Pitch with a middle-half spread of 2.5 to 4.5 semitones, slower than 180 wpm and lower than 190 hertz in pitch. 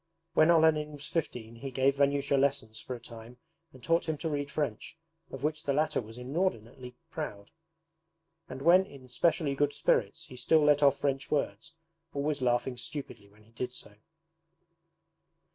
Yes: average, 3.5 semitones; average, 165 wpm; medium, 140 Hz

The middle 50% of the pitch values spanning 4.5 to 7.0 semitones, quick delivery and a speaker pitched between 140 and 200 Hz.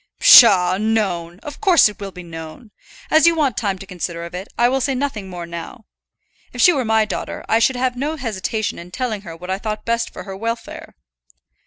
No: wide, 5.6 semitones; fast, 215 wpm; high, 215 Hz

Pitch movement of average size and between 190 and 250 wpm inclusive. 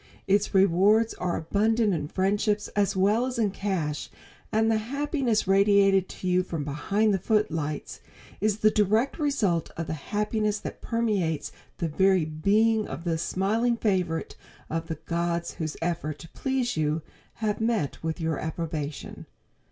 No: average, 4.8 semitones; average, 150 wpm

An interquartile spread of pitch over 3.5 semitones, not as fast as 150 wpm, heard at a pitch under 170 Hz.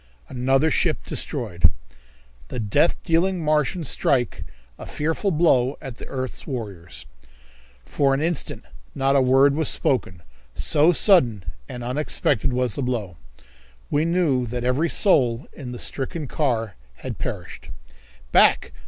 Yes: average, 4.0 semitones; slow, 135 wpm; low, 135 Hz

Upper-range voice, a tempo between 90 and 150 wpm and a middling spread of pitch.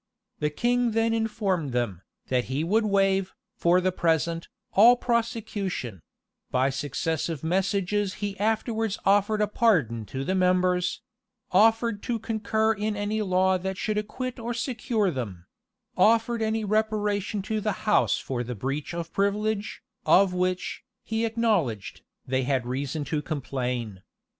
No: high, 195 Hz; average, 140 wpm; wide, 6.4 semitones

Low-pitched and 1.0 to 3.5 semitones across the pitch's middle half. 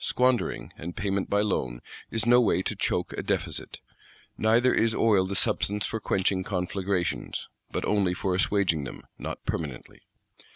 Yes: low, 100 Hz; average, 3.2 semitones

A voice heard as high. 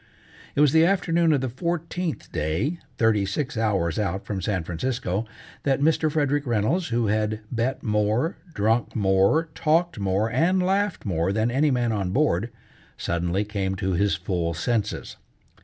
No: low, 115 Hz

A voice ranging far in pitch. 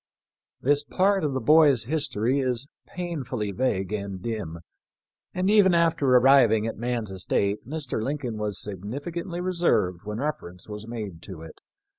Yes: wide, 6.4 semitones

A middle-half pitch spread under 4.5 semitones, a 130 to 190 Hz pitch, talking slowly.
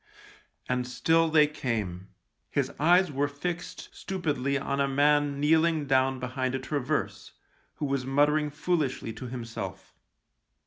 Yes: average, 2.9 semitones; medium, 140 Hz; slow, 130 wpm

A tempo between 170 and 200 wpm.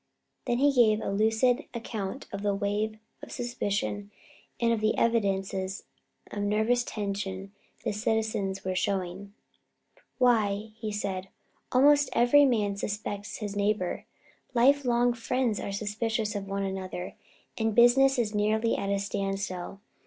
No: average, 140 wpm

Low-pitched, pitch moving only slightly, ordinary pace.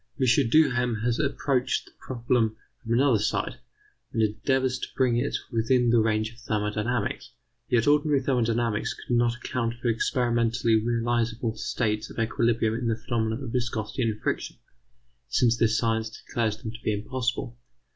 Yes: low, 115 Hz; narrow, 1.8 semitones; average, 155 wpm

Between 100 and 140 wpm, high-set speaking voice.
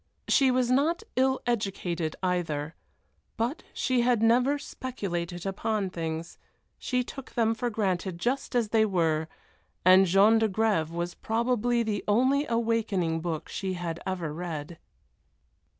Yes: slow, 135 wpm; high, 205 Hz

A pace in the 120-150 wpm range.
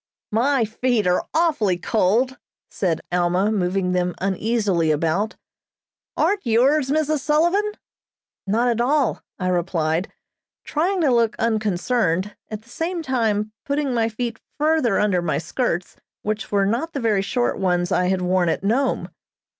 Yes: average, 145 wpm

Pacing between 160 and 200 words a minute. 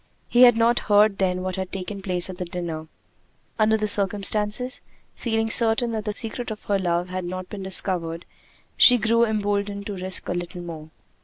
Yes: average, 185 wpm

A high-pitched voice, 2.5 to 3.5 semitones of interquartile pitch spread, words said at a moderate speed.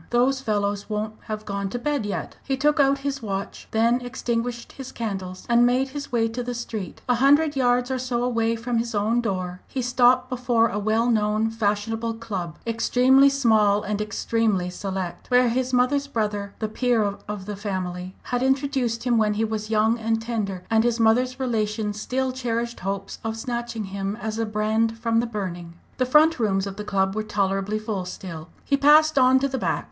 Yes: high, 225 Hz; average, 3.1 semitones; average, 195 wpm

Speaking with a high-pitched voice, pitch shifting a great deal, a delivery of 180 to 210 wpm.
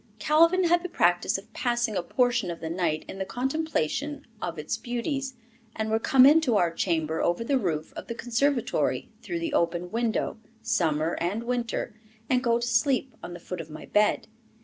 Yes: high, 230 Hz; wide, 7.4 semitones; average, 190 wpm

